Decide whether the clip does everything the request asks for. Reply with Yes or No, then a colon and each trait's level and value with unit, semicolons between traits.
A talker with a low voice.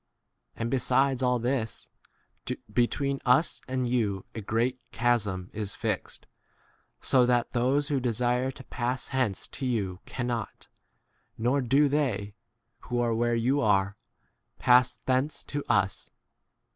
Yes: low, 125 Hz